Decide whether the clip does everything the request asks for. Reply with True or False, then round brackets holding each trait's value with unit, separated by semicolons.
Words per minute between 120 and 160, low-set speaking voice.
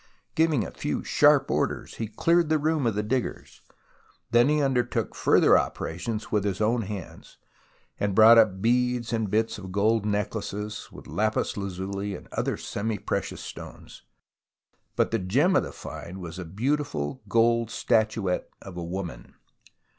True (155 wpm; 110 Hz)